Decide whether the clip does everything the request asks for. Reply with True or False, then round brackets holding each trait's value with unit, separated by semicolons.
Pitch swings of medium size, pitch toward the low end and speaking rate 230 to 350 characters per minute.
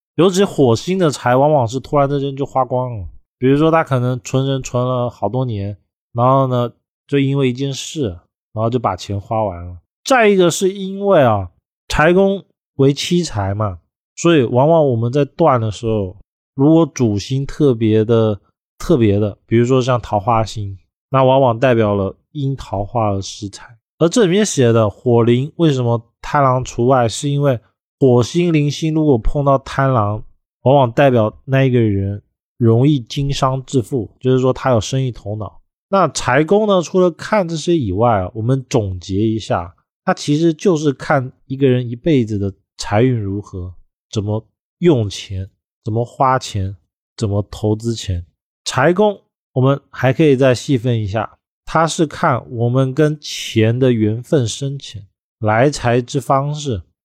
True (5.0 semitones; 125 Hz; 240 characters per minute)